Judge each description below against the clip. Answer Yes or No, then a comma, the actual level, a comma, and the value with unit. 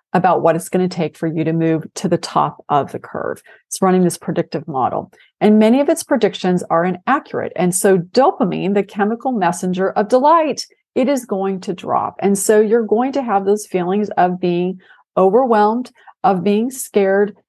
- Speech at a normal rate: Yes, average, 190 wpm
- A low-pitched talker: No, high, 200 Hz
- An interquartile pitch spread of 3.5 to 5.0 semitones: Yes, average, 4.3 semitones